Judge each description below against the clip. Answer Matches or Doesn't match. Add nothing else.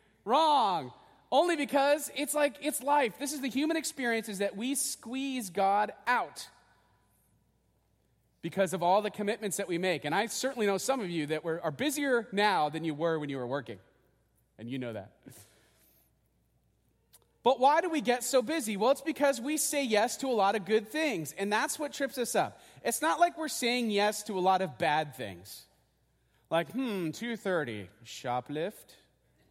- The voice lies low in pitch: Doesn't match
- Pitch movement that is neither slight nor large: Doesn't match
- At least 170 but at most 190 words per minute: Matches